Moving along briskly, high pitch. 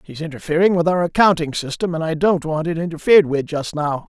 No: fast, 215 wpm; medium, 165 Hz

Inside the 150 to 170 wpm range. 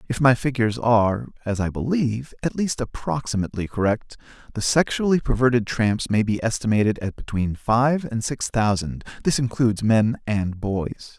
Yes: average, 155 wpm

